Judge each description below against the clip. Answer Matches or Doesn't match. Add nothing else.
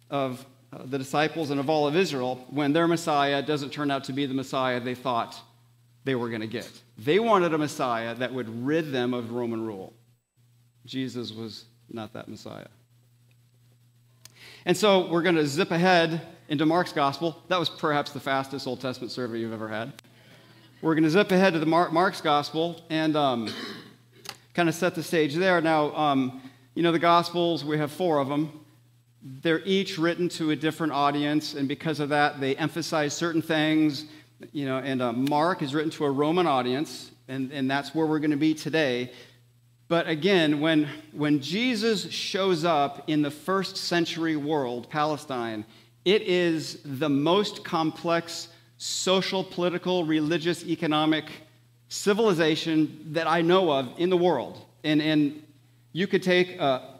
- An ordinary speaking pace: Matches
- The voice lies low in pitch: Doesn't match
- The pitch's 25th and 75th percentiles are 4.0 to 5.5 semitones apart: Matches